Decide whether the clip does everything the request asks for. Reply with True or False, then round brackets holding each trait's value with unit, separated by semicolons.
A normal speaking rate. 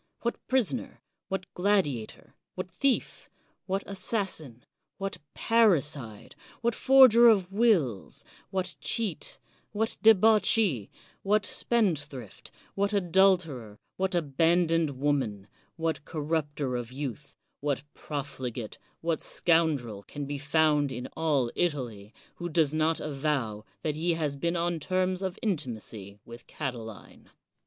False (120 wpm)